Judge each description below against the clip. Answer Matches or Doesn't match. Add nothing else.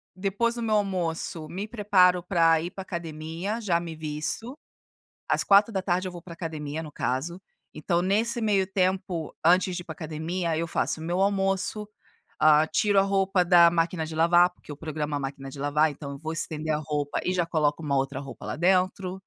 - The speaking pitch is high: Doesn't match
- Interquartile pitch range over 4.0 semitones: Doesn't match